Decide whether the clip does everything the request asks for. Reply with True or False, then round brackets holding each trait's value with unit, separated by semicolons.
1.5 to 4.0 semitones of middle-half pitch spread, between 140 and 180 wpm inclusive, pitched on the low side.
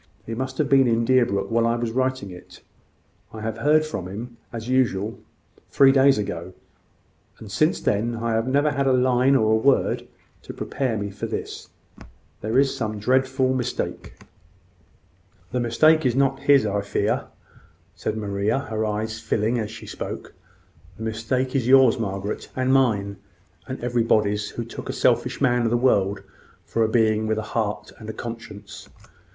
True (3.3 semitones; 170 wpm; 115 Hz)